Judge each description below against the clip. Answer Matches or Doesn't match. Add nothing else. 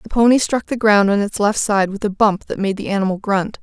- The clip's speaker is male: Doesn't match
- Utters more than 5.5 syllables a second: Matches